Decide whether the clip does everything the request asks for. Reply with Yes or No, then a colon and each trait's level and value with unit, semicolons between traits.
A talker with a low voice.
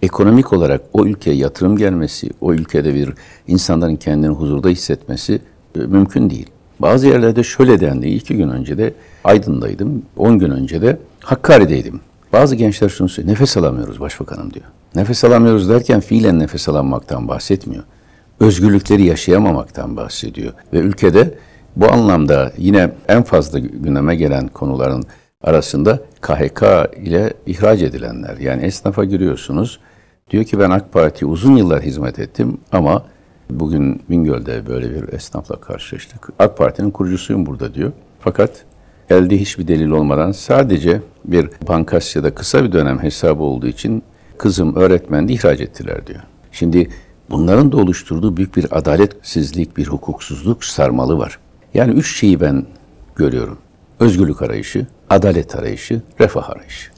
Yes: very low, 90 Hz